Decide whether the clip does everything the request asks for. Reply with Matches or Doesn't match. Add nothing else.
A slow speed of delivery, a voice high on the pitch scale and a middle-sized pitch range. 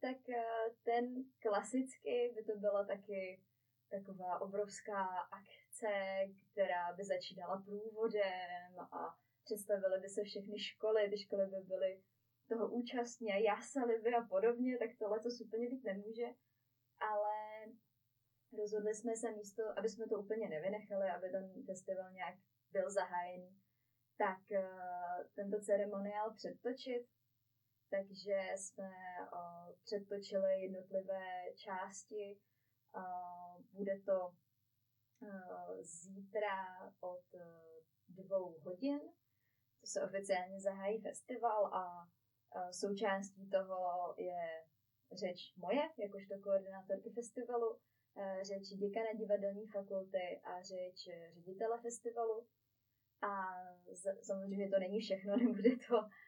Matches